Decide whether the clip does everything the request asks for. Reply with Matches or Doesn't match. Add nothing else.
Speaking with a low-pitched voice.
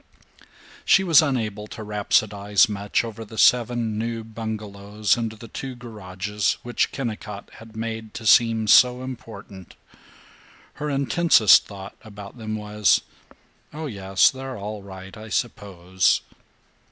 Matches